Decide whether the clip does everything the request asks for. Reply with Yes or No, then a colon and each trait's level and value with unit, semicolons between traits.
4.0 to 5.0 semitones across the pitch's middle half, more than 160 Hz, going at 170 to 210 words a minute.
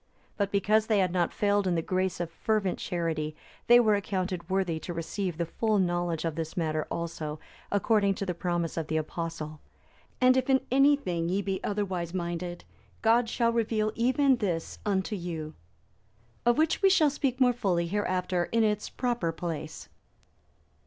Yes: average, 4.6 semitones; medium, 185 Hz; average, 175 wpm